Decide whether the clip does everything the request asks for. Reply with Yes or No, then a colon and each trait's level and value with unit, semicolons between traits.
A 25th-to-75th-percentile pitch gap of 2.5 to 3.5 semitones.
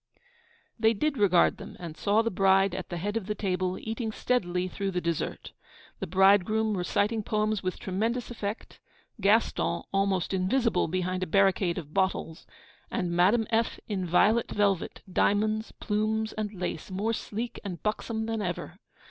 Yes: average, 3.1 semitones